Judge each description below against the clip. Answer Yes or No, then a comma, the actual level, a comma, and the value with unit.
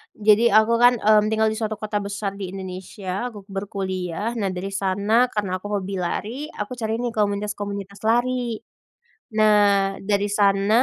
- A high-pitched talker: Yes, high, 205 Hz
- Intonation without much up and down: Yes, narrow, 1.7 semitones